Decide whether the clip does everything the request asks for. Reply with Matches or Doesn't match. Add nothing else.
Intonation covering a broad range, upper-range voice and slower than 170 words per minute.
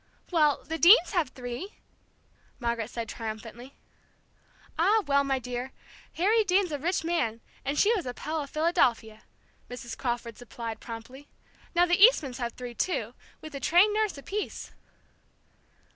Matches